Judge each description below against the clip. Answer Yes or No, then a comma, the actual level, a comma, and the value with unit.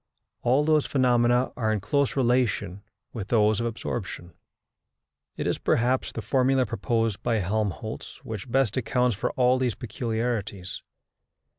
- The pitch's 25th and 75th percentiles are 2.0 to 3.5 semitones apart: Yes, average, 2.9 semitones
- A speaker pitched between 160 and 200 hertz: No, low, 120 Hz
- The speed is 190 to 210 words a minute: No, slow, 135 wpm